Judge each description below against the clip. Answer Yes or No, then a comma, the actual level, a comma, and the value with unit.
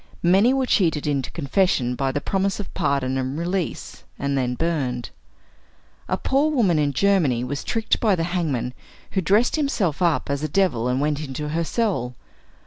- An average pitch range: No, wide, 6.2 semitones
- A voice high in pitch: No, medium, 160 Hz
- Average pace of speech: Yes, average, 175 wpm